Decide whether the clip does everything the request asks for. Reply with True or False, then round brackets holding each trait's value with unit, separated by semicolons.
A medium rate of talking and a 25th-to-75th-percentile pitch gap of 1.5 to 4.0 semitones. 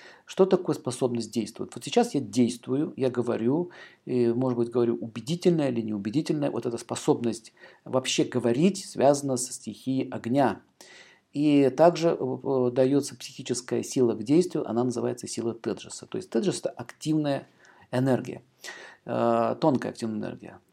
True (135 wpm; 3.6 semitones)